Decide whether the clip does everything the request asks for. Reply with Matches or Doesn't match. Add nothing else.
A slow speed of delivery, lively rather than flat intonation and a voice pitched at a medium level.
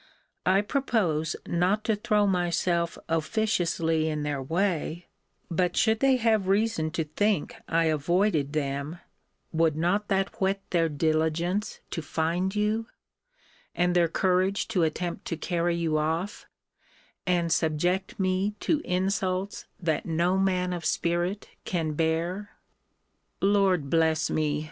Doesn't match